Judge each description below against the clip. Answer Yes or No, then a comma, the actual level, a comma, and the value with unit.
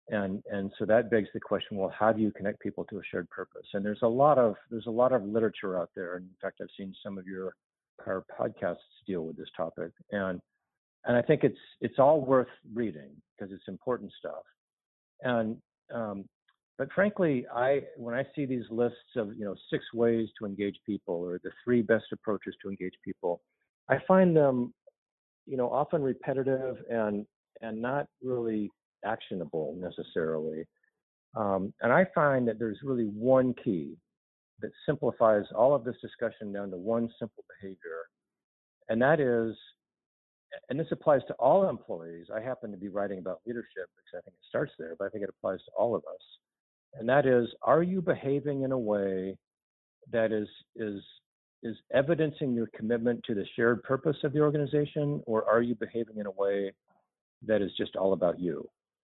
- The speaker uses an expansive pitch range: No, average, 4.4 semitones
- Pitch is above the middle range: No, low, 115 Hz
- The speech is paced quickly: No, average, 185 wpm